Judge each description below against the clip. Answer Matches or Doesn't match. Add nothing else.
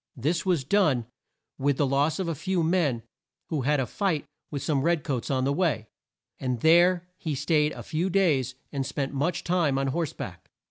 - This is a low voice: Doesn't match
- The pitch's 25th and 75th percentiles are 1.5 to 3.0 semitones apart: Doesn't match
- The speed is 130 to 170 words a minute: Doesn't match